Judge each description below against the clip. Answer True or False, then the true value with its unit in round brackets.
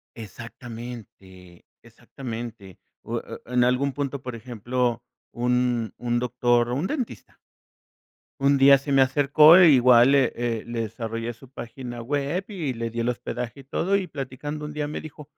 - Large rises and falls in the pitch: False (3.1 semitones)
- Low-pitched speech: True (125 Hz)